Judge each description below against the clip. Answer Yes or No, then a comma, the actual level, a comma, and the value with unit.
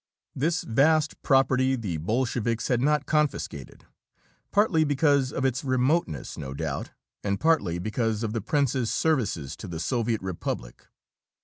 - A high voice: No, low, 125 Hz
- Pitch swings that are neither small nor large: No, wide, 6.1 semitones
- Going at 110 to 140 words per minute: Yes, slow, 135 wpm